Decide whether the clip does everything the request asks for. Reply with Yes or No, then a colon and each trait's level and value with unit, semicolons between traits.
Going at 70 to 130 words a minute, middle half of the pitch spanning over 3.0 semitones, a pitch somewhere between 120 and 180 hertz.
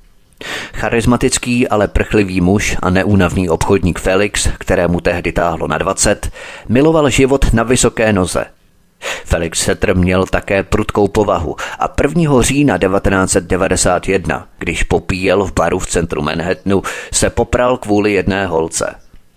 No: average, 125 wpm; average, 4.0 semitones; low, 100 Hz